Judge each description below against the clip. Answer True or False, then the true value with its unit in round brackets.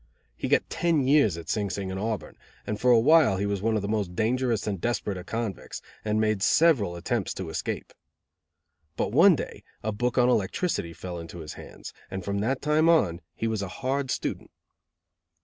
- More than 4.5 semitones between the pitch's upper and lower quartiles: True (5.1 semitones)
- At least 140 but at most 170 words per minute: False (200 wpm)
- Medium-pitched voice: False (110 Hz)